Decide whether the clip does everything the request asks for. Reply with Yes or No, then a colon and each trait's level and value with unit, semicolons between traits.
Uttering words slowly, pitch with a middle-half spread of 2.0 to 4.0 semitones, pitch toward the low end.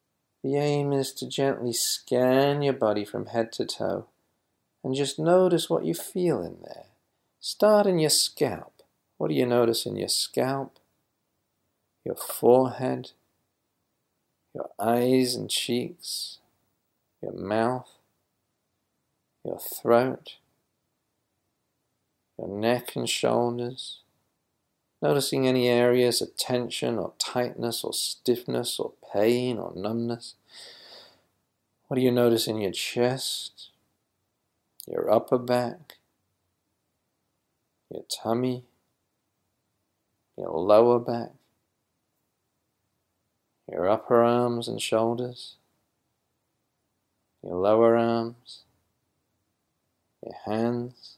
Yes: slow, 95 wpm; narrow, 2.6 semitones; low, 120 Hz